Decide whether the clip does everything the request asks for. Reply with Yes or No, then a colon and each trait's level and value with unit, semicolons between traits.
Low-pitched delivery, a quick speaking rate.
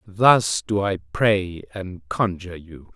No: very low, 95 Hz; average, 140 wpm